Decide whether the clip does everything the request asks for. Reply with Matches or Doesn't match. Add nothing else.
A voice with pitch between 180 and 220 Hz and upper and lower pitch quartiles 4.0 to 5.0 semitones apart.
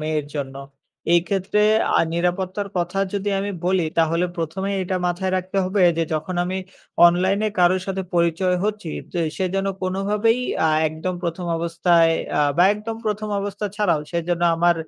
Doesn't match